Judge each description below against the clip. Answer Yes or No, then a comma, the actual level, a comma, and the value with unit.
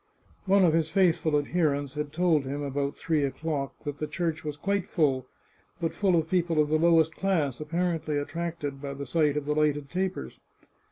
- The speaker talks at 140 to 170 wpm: No, average, 200 wpm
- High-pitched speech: No, medium, 155 Hz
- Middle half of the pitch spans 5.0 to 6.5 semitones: No, average, 2.8 semitones